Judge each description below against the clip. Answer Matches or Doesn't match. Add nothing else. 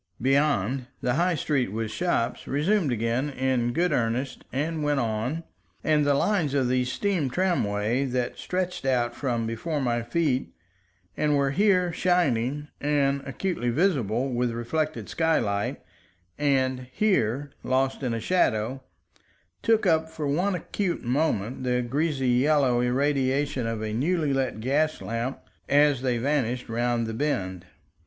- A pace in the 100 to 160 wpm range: Matches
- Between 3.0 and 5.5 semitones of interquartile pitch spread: Matches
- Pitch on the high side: Doesn't match